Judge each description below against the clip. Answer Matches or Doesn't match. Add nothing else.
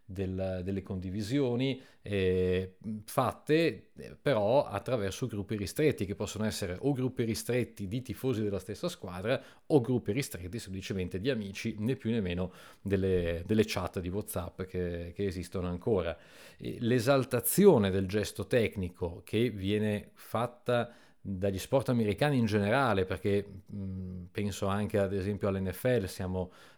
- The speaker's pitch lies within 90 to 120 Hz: Matches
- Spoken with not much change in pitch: Doesn't match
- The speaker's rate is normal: Matches